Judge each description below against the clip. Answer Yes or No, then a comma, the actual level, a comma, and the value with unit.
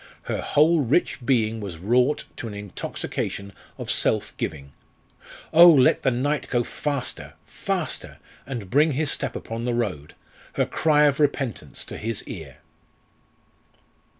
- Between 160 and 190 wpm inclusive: No, average, 140 wpm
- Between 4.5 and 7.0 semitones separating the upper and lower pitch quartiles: Yes, average, 5.1 semitones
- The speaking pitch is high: No, low, 125 Hz